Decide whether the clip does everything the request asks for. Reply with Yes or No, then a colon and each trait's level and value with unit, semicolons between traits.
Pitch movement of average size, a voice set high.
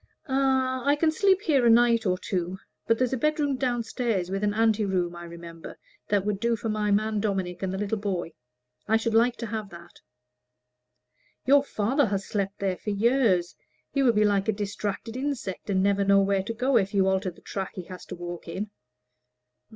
Yes: average, 3.8 semitones; high, 210 Hz